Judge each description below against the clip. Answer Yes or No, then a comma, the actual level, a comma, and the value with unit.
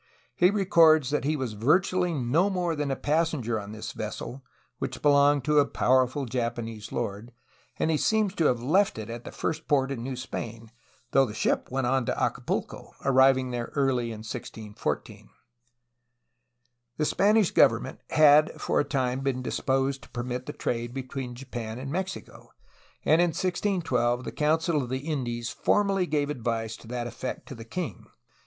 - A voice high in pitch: No, low, 135 Hz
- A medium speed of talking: Yes, average, 175 wpm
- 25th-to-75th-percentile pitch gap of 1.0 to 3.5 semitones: No, average, 4.5 semitones